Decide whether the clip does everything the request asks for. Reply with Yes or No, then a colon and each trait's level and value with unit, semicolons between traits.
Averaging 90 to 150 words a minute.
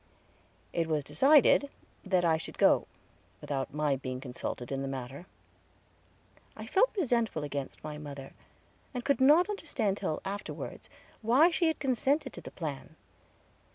Yes: average, 140 wpm